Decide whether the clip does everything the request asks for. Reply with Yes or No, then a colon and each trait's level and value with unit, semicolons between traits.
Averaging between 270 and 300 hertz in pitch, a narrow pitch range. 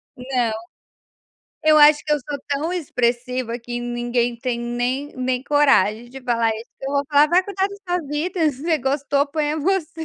No: very high, 280 Hz; average, 4.0 semitones